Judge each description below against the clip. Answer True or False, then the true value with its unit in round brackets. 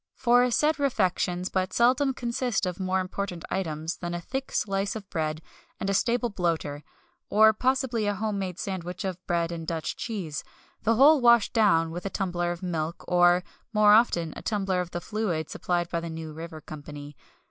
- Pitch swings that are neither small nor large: True (4.5 semitones)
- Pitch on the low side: False (185 Hz)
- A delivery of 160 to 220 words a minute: True (185 wpm)